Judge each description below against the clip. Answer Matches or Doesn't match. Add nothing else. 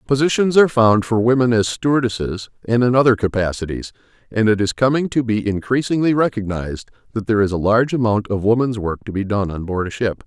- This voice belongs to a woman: Doesn't match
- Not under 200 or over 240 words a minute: Matches